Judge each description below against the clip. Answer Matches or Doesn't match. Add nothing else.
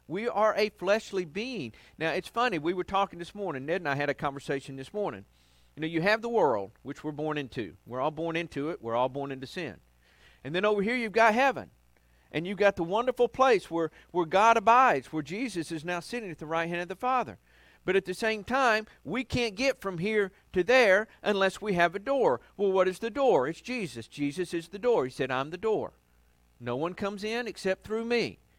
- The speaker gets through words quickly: Matches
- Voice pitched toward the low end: Doesn't match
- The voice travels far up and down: Matches